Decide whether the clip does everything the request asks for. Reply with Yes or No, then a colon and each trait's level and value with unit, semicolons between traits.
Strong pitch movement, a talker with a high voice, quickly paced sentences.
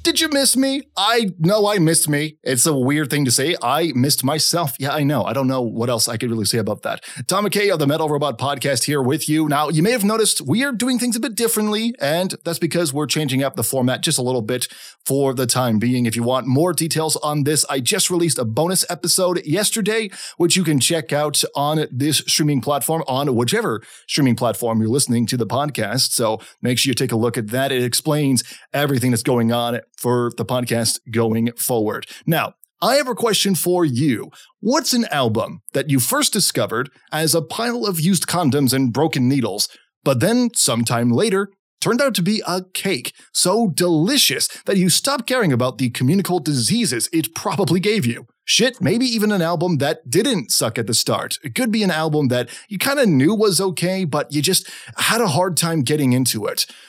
No: wide, 6.8 semitones; medium, 150 Hz; fast, 215 wpm